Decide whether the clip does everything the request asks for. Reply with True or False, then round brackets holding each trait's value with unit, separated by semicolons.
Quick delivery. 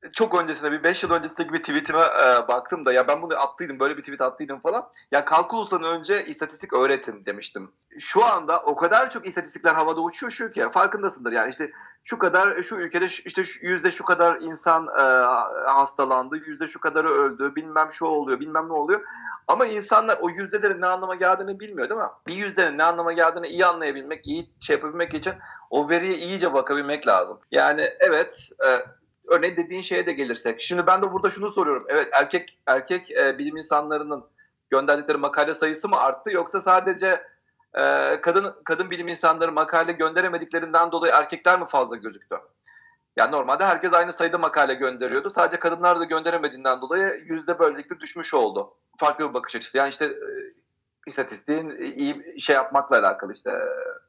True (175 wpm)